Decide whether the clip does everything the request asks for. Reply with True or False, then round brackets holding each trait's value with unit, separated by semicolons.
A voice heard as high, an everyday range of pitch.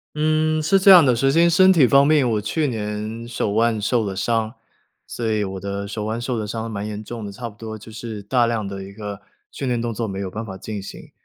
False (110 Hz; 3.3 semitones)